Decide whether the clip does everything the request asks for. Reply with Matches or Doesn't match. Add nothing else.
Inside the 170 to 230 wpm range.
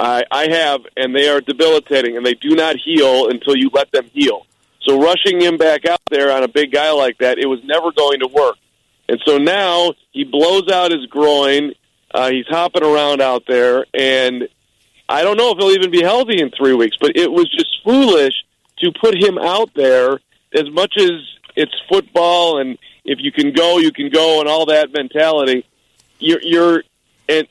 Matches